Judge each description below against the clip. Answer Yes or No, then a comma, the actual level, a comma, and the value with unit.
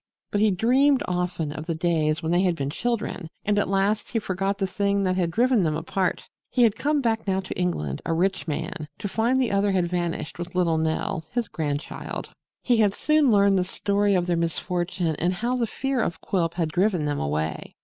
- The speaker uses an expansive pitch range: No, average, 4.1 semitones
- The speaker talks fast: Yes, fast, 215 wpm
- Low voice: No, medium, 185 Hz